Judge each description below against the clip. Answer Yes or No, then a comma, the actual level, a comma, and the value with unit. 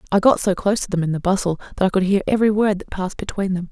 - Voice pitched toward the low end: No, high, 195 Hz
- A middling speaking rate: No, fast, 305 wpm